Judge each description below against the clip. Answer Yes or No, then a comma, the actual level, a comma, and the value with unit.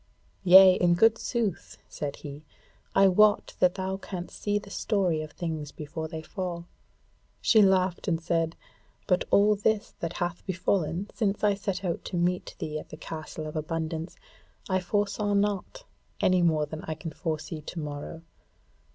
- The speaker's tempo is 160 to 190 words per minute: Yes, average, 165 wpm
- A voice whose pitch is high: No, medium, 175 Hz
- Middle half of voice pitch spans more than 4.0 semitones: No, average, 3.7 semitones